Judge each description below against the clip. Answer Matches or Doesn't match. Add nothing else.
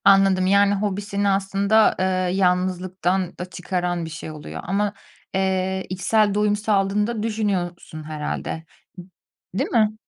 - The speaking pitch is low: Doesn't match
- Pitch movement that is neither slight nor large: Doesn't match